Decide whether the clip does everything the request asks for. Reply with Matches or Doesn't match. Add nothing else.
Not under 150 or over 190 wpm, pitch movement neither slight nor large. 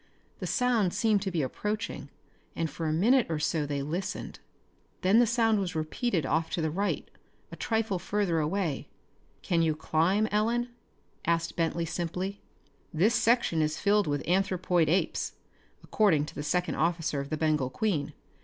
Matches